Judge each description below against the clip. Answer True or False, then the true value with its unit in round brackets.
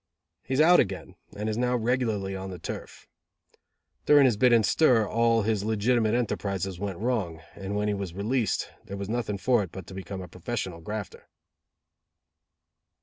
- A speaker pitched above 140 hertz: False (105 Hz)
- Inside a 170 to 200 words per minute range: True (175 wpm)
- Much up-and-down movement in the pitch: False (3.7 semitones)